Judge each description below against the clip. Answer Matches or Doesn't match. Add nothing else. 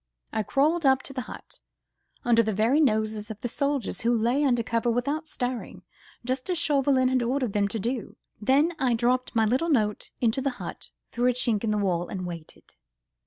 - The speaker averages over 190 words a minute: Matches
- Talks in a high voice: Matches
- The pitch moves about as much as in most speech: Matches